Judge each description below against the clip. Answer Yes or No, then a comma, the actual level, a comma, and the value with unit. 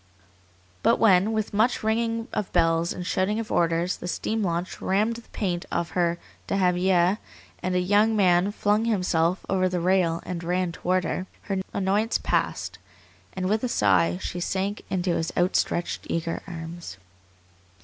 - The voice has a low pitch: No, medium, 185 Hz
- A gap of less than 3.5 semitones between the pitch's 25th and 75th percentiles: Yes, average, 3.0 semitones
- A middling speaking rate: Yes, average, 160 wpm